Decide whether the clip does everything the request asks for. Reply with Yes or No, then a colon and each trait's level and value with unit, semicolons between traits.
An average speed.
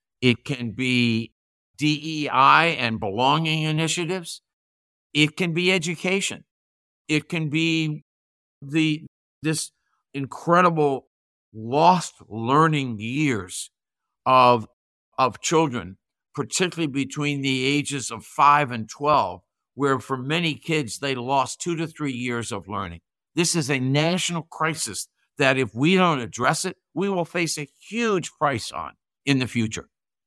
No: slow, 125 wpm